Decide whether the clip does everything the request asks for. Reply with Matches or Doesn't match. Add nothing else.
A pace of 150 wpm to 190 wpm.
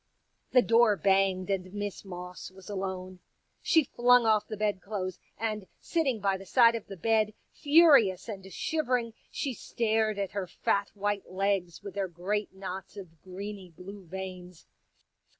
Matches